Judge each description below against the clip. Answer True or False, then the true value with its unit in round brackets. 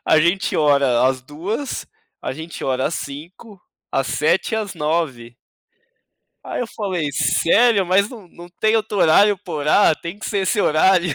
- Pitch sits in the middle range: True (170 Hz)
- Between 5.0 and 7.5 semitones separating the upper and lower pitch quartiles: True (5.4 semitones)